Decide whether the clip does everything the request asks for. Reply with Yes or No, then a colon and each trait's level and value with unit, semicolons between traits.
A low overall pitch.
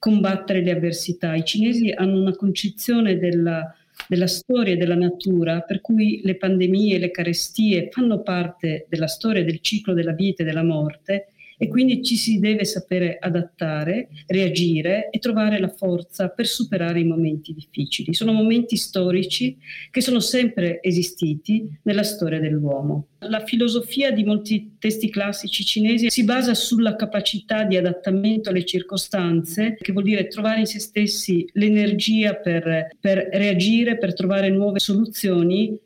No: high, 195 Hz